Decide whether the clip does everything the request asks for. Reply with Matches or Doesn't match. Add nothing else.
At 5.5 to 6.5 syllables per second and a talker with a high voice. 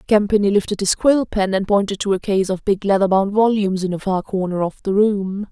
Matches